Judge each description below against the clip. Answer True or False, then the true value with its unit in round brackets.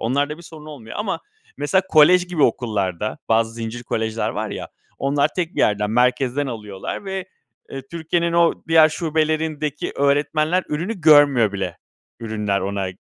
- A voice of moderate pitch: True (145 Hz)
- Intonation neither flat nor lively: False (6.2 semitones)